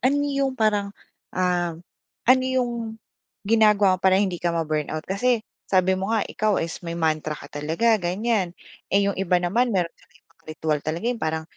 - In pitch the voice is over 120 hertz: Yes, high, 190 Hz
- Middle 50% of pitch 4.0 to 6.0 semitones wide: Yes, average, 5.1 semitones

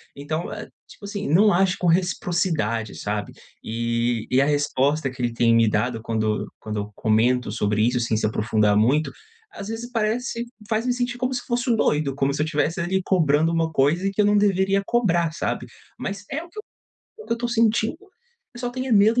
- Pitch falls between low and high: Yes, medium, 165 Hz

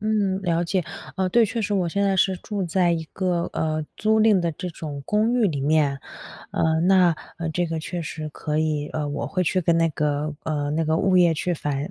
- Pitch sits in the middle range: Yes, medium, 170 Hz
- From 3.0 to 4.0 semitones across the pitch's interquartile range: Yes, average, 3.6 semitones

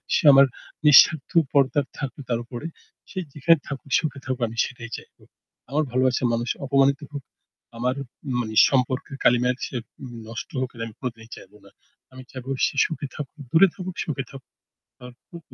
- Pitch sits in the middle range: No, low, 130 Hz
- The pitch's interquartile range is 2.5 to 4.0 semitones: Yes, average, 2.8 semitones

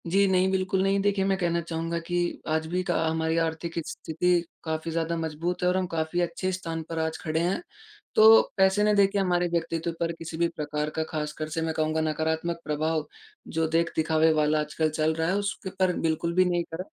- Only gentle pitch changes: Yes, narrow, 2.1 semitones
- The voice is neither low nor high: Yes, medium, 165 Hz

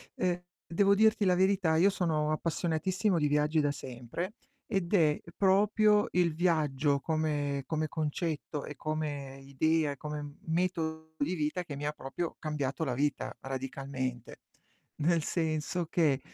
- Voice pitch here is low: No, medium, 155 Hz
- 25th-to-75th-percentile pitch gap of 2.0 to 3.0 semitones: No, average, 3.4 semitones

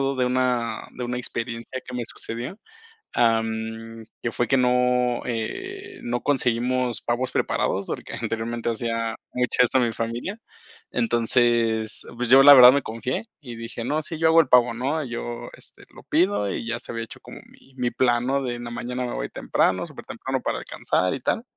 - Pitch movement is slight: Yes, narrow, 1.7 semitones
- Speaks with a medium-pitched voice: No, low, 120 Hz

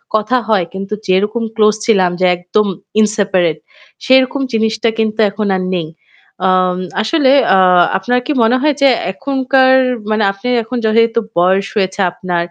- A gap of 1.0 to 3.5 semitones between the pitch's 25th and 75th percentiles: No, average, 4.1 semitones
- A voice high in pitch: Yes, high, 215 Hz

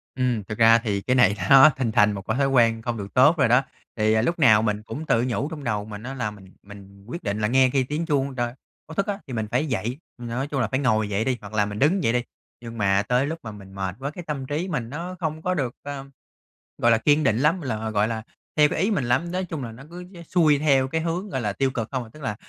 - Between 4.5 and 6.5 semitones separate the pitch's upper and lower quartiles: Yes, average, 5.2 semitones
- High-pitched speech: No, low, 125 Hz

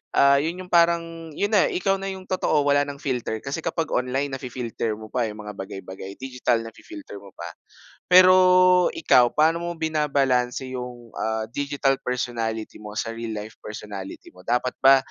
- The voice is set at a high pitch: No, low, 130 Hz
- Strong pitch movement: Yes, wide, 6.1 semitones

